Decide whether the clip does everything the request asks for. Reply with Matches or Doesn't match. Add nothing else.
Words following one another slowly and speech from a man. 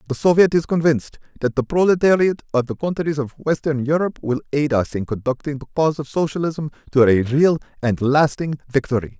Doesn't match